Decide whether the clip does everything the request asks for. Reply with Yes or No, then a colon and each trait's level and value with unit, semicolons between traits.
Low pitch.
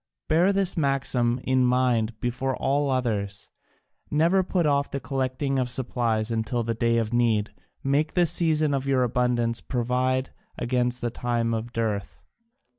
Yes: low, 125 Hz